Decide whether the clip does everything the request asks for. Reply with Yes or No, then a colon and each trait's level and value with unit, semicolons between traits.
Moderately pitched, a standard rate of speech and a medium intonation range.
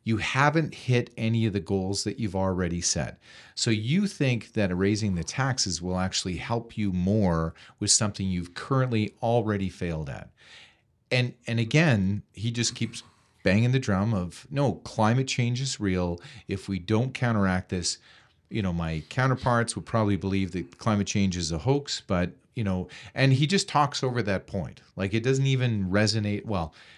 No: low, 105 Hz; average, 175 wpm; average, 4.3 semitones